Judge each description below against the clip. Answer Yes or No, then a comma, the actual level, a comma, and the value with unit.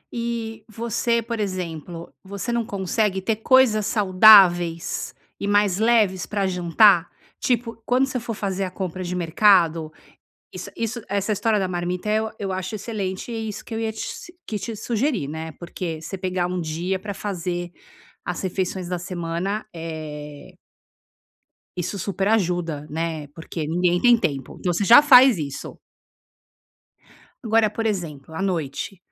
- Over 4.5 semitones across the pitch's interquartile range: No, average, 4.1 semitones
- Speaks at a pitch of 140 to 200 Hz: Yes, high, 190 Hz